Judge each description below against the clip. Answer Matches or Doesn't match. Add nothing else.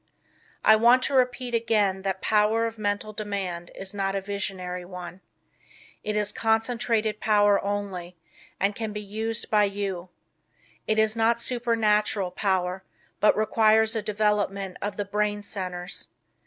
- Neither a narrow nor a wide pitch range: Doesn't match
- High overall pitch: Matches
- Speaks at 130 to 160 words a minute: Matches